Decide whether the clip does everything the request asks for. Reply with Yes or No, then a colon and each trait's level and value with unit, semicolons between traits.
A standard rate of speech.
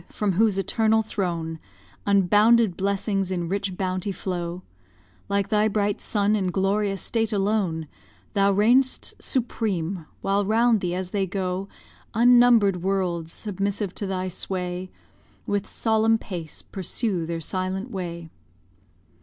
No: slow, 125 wpm